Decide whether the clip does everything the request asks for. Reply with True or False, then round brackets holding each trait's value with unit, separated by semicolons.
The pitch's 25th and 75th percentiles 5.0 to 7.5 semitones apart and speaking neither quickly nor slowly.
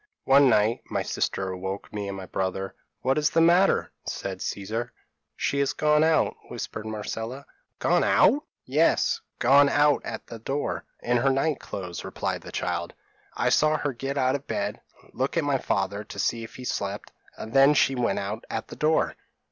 True (5.4 semitones; 190 wpm)